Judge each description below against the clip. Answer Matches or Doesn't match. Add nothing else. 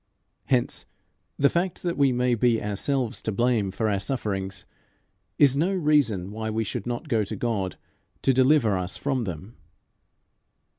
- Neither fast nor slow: Matches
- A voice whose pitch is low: Matches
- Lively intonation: Doesn't match